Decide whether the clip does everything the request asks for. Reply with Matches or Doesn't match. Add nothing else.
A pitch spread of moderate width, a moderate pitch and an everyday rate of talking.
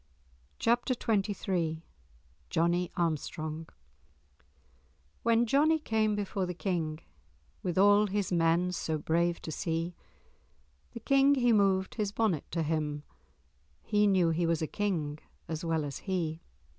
Doesn't match